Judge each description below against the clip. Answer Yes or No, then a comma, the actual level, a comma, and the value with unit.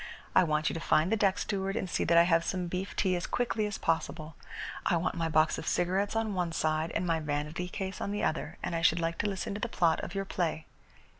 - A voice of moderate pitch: Yes, medium, 175 Hz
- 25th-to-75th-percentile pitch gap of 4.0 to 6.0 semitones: No, average, 3.1 semitones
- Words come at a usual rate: No, fast, 255 wpm